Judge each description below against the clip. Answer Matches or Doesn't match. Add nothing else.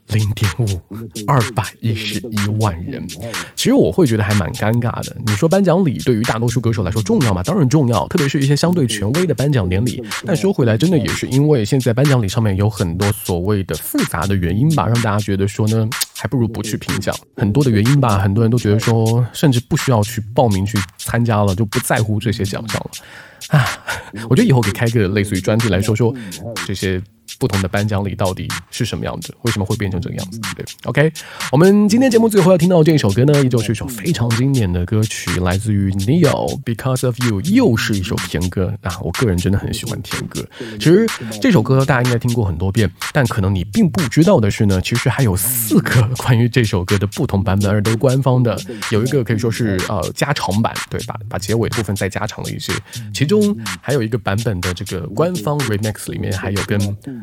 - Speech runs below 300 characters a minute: Doesn't match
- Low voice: Matches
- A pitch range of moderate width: Matches